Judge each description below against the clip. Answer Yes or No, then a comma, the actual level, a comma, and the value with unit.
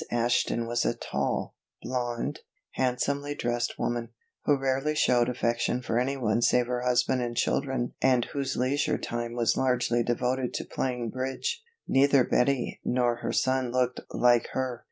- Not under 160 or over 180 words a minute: No, average, 150 wpm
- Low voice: Yes, low, 125 Hz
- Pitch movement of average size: No, narrow, 1.7 semitones